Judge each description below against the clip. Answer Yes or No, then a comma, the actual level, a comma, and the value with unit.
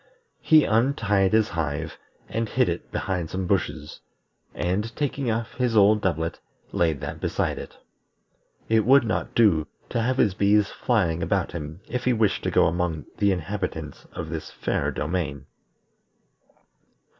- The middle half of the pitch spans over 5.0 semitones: Yes, wide, 5.5 semitones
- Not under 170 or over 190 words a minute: No, average, 150 wpm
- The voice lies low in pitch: Yes, low, 100 Hz